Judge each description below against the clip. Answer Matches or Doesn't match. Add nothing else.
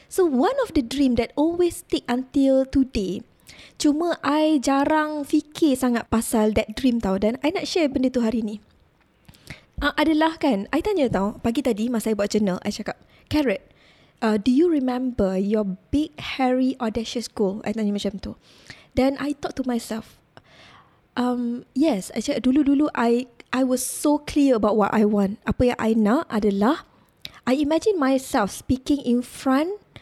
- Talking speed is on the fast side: Matches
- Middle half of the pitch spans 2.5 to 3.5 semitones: Doesn't match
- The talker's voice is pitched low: Doesn't match